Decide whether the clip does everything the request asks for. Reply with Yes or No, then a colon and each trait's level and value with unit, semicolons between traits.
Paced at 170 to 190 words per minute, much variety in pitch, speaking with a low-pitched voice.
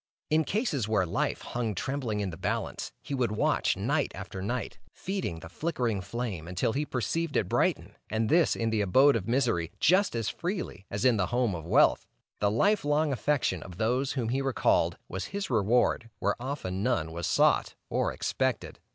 Yes: average, 185 wpm; wide, 6.0 semitones; low, 115 Hz